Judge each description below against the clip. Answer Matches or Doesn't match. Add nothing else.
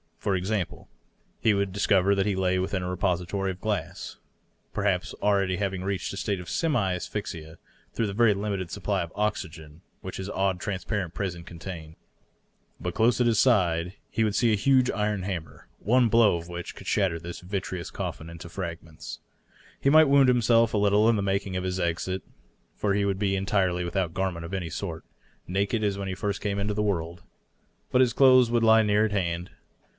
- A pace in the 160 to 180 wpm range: Doesn't match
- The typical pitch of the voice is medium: Doesn't match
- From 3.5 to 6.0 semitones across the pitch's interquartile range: Doesn't match